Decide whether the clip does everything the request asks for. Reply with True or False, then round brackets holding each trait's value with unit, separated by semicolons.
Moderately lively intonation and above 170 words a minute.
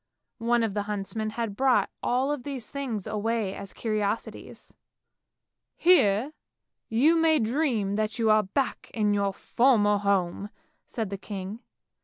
False (3.4 semitones; 145 wpm)